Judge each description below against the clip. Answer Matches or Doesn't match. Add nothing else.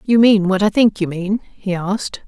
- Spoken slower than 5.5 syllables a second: Matches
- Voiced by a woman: Matches